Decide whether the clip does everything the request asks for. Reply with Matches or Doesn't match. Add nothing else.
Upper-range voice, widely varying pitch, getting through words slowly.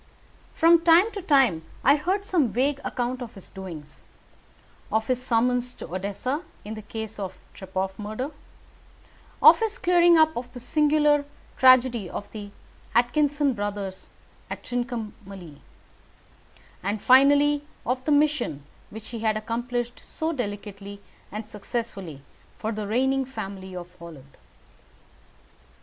Matches